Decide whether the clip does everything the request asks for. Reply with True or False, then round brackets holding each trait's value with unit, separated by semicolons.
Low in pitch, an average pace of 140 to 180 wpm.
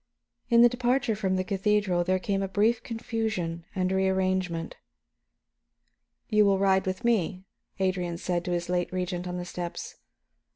False (190 Hz; 155 wpm)